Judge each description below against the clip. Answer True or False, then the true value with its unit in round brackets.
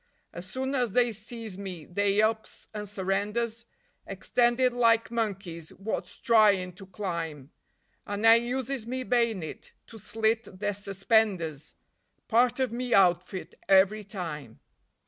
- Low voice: False (210 Hz)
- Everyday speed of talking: False (125 wpm)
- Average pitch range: True (3.8 semitones)